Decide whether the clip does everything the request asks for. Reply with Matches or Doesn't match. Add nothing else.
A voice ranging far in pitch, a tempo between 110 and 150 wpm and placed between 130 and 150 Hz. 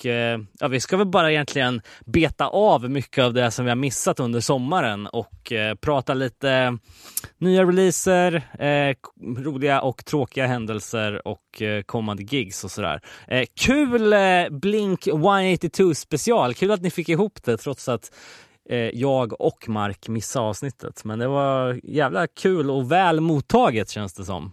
Matches